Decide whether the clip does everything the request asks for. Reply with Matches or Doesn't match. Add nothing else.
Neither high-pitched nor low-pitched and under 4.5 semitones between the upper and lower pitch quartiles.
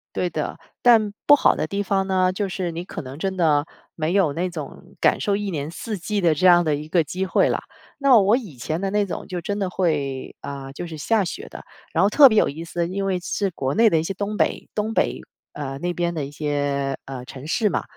Doesn't match